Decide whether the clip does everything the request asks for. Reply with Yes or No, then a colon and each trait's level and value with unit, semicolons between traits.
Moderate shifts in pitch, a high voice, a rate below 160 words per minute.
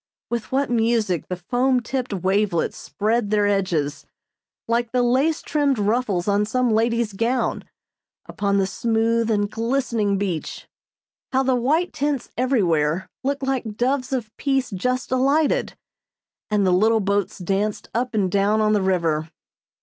Yes: average, 4.1 semitones; high, 225 Hz; average, 145 wpm